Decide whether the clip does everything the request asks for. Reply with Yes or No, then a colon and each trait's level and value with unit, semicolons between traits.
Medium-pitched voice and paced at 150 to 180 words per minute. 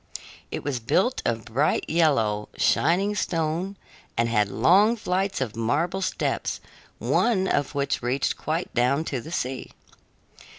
No: medium, 150 Hz; slow, 135 wpm